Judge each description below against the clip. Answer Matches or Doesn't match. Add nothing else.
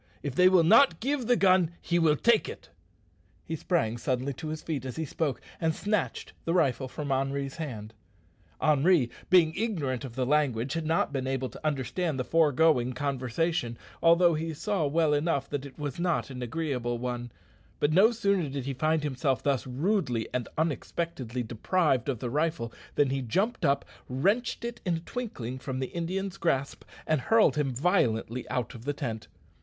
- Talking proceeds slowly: Doesn't match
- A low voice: Doesn't match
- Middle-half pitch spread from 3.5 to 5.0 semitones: Matches